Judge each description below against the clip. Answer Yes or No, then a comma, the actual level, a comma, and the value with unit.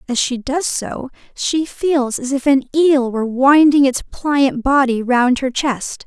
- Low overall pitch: No, very high, 265 Hz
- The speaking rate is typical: Yes, average, 180 wpm